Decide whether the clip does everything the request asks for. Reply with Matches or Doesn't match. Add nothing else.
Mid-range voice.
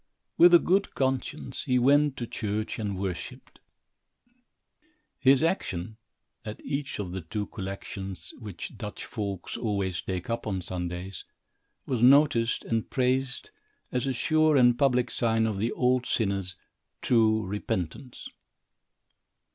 Doesn't match